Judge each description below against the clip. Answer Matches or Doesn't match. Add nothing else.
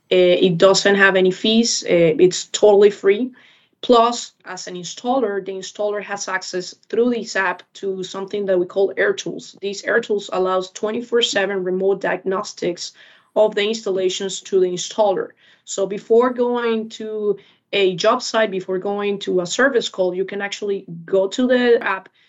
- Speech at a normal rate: Matches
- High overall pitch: Matches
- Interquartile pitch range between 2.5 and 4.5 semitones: Matches